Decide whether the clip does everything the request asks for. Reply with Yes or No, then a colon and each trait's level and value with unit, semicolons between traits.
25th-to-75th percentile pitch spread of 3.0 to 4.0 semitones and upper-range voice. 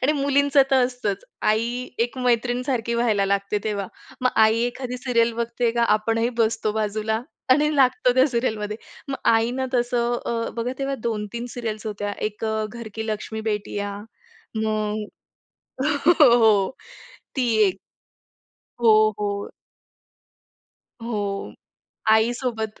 No: narrow, 2.4 semitones; high, 230 Hz